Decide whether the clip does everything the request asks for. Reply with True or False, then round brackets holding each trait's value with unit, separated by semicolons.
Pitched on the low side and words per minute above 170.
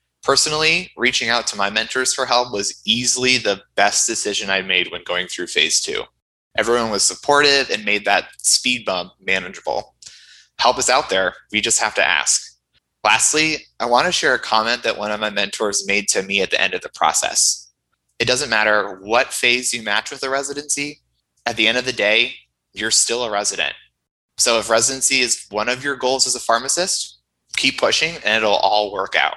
True (120 Hz; 200 wpm)